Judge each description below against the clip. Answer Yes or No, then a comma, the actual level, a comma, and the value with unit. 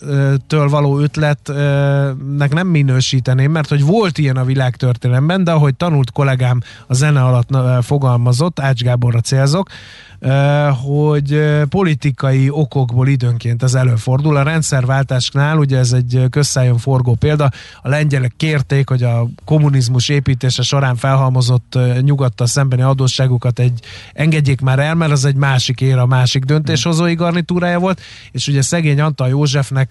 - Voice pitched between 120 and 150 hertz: Yes, low, 135 Hz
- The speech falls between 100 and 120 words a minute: No, average, 135 wpm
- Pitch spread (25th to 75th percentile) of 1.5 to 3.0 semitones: Yes, narrow, 2.5 semitones